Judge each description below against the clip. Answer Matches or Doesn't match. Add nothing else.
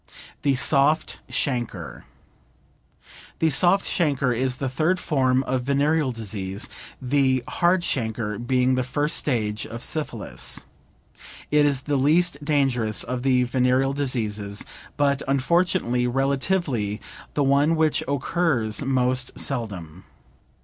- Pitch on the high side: Doesn't match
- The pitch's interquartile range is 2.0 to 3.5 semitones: Matches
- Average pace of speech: Doesn't match